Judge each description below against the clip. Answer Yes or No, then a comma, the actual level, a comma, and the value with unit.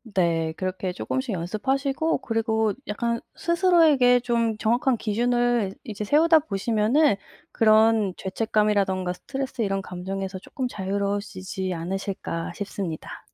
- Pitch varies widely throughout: No, average, 4.3 semitones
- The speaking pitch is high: Yes, high, 215 Hz